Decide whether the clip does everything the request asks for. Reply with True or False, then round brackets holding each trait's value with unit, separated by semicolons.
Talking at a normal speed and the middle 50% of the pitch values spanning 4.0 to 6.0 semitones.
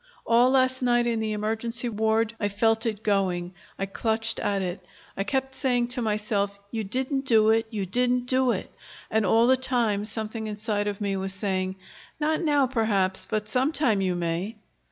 False (180 wpm; 3.3 semitones)